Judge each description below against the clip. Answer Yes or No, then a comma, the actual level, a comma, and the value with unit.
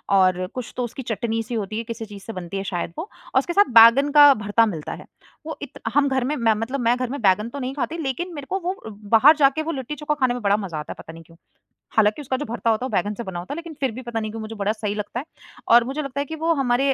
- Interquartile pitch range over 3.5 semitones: Yes, average, 4.9 semitones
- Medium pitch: No, high, 235 Hz